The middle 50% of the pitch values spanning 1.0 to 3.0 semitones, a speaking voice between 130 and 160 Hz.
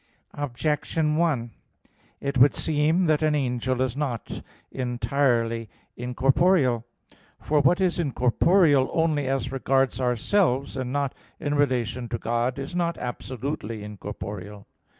No: average, 3.6 semitones; low, 135 Hz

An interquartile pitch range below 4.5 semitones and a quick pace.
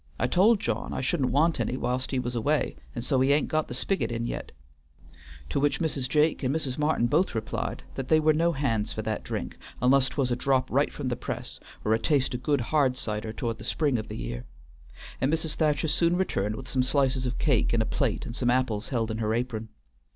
Yes: average, 4.1 semitones; fast, 235 wpm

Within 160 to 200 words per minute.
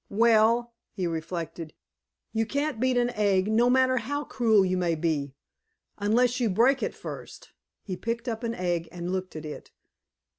Yes: average, 170 wpm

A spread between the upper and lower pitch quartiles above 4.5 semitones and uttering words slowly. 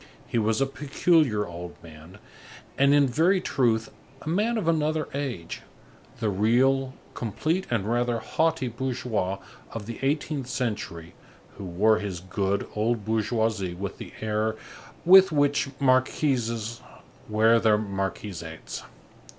Yes: average, 4.9 semitones; slow, 125 wpm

